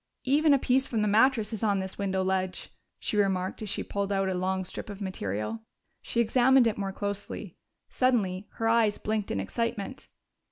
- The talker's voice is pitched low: No, high, 205 Hz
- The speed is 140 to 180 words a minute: No, average, 190 wpm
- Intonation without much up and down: No, average, 3.4 semitones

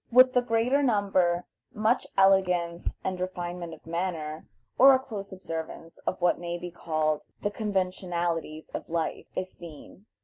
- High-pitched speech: No, medium, 180 Hz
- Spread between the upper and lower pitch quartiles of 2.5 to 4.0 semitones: Yes, average, 3.3 semitones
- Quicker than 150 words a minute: No, average, 145 wpm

